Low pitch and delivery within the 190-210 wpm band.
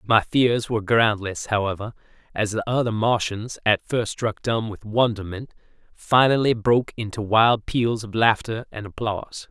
No: low, 110 Hz; average, 150 wpm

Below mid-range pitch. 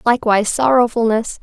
No: high, 230 Hz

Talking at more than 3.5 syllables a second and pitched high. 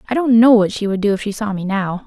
Yes: 6.4 syllables/s; high, 210 Hz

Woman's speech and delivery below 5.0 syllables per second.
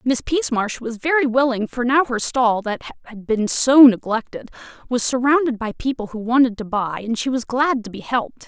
No: female; 5.1 syllables/s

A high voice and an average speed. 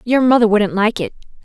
No: high, 220 Hz; fast, 210 wpm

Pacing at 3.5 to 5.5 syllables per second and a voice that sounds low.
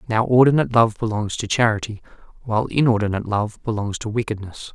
No: 6.4 syllables/s; low, 110 Hz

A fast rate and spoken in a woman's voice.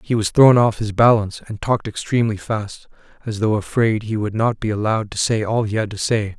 No: fast, 235 wpm; male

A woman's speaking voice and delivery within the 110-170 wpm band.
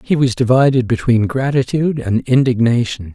No: male; slow, 135 wpm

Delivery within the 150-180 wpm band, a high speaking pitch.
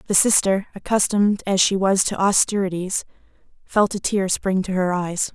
Yes: average, 170 wpm; high, 195 Hz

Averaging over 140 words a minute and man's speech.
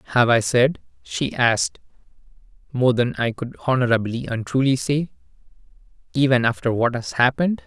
No: slow, 135 wpm; male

